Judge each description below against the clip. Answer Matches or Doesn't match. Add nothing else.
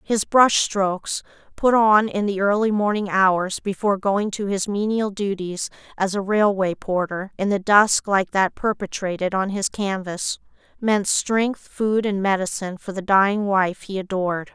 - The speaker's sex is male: Doesn't match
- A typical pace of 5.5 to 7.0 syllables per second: Doesn't match